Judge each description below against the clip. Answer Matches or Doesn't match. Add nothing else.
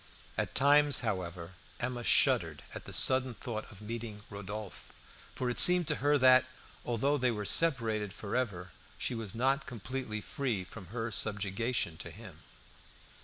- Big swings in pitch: Doesn't match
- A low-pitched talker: Matches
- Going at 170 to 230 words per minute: Doesn't match